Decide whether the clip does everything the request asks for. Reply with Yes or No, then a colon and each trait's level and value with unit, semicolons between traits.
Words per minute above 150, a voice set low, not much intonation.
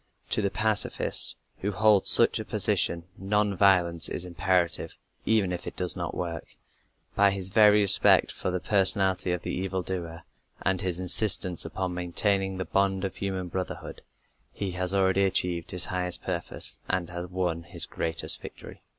Yes: average, 165 wpm; very low, 95 Hz; narrow, 1.7 semitones